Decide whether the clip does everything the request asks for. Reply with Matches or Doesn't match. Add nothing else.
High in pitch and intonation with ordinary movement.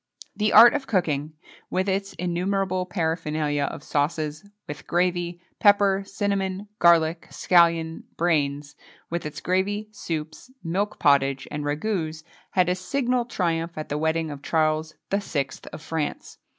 Doesn't match